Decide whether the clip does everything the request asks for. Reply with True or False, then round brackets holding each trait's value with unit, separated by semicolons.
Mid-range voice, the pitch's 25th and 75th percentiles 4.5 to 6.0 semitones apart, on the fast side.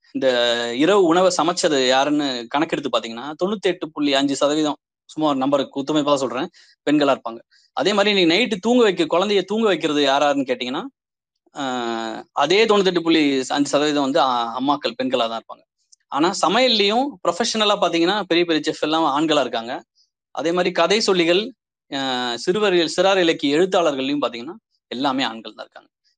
True (155 Hz; 5.5 semitones; 145 wpm)